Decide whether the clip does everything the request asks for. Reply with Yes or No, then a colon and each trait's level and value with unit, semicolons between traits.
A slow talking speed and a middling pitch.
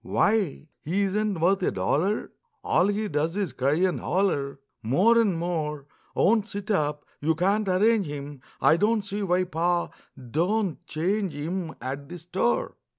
No: average, 155 wpm; medium, 180 Hz